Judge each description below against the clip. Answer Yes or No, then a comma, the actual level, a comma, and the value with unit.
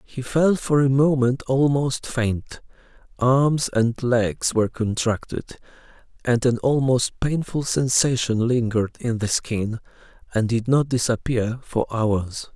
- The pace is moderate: No, slow, 130 wpm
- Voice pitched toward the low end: Yes, low, 125 Hz